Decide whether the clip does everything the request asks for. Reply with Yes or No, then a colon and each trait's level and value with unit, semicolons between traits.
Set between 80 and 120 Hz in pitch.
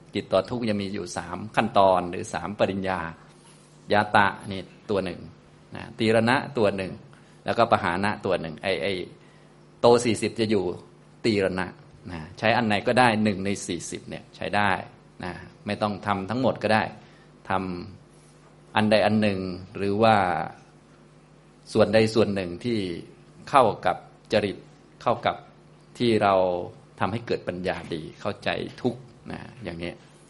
Yes: low, 105 Hz